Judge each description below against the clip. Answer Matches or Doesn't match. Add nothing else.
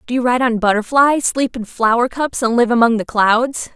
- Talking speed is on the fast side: Matches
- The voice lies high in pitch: Matches